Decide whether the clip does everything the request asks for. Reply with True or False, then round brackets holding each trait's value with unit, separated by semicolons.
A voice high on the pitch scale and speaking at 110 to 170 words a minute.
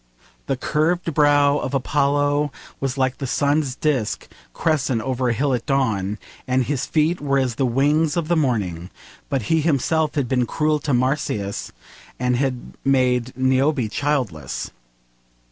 False (135 Hz; 150 wpm)